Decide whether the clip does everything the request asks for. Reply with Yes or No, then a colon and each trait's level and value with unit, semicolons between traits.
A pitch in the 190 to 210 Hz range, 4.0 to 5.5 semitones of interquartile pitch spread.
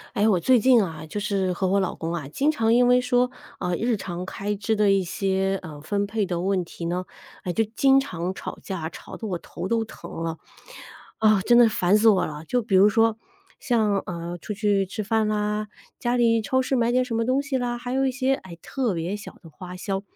Yes: high, 205 Hz; average, 4.4 semitones